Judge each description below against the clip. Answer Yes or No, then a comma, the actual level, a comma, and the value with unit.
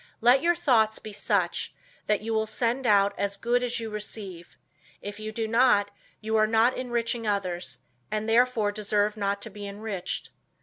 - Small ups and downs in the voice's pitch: Yes, narrow, 2.3 semitones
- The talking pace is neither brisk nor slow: Yes, average, 175 wpm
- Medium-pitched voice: No, high, 215 Hz